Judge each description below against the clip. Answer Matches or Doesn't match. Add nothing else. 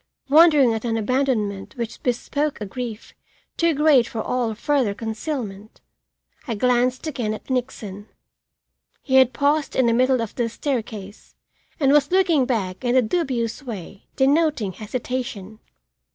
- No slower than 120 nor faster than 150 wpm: Matches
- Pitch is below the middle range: Doesn't match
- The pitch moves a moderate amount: Matches